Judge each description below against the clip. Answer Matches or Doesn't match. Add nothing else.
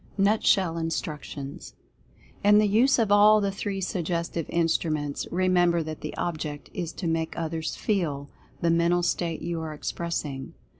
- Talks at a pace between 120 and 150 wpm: Matches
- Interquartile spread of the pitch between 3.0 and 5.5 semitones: Matches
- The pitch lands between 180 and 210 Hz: Doesn't match